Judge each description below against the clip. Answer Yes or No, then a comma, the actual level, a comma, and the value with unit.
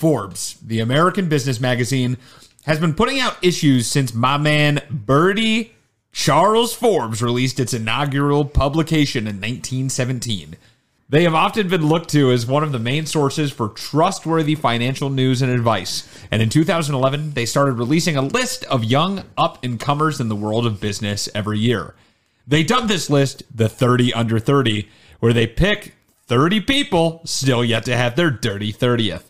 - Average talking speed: Yes, average, 165 wpm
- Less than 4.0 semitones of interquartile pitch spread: No, average, 5.0 semitones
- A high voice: No, low, 135 Hz